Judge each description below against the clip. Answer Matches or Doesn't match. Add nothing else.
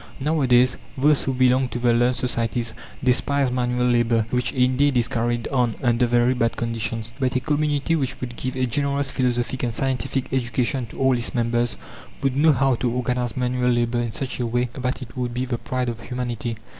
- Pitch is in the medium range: Doesn't match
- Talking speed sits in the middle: Matches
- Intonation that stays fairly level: Matches